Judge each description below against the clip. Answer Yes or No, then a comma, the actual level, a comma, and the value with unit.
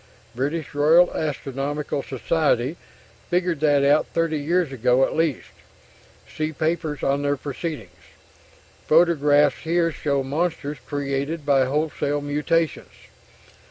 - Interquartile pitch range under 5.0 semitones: Yes, narrow, 2.6 semitones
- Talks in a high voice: No, medium, 145 Hz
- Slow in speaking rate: Yes, slow, 110 wpm